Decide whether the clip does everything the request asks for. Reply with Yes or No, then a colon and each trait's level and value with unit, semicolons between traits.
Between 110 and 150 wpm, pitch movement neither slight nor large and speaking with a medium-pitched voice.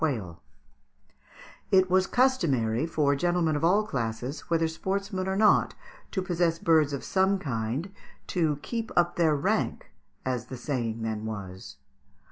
No: average, 140 wpm; wide, 6.9 semitones; medium, 160 Hz